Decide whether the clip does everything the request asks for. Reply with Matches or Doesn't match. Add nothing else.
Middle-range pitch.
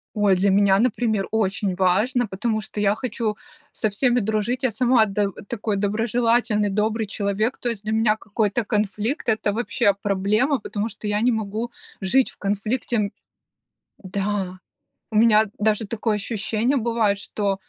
Doesn't match